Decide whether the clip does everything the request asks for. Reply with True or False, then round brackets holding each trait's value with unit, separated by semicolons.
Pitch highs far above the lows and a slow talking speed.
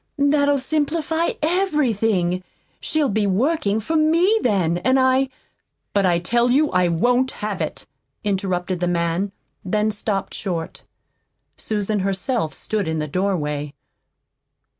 True (7.1 semitones; 130 wpm)